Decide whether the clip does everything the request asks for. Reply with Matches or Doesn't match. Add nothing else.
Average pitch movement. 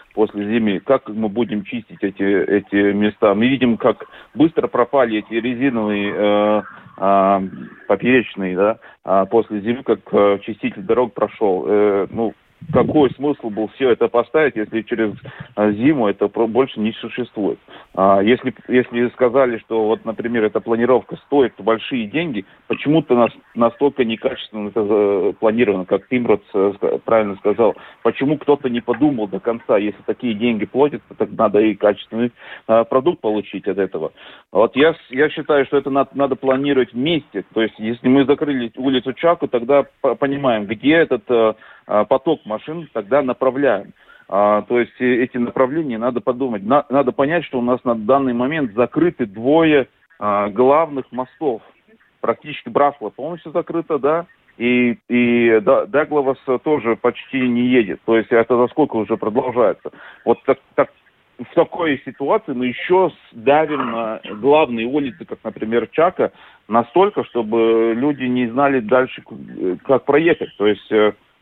Matches